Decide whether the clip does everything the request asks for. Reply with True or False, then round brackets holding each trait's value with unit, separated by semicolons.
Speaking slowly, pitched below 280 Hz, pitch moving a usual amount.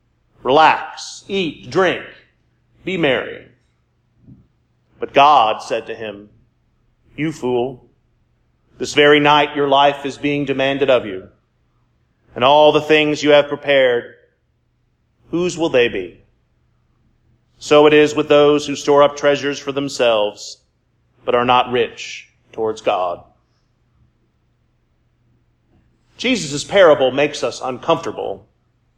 True (115 wpm; 140 Hz; 3.5 semitones)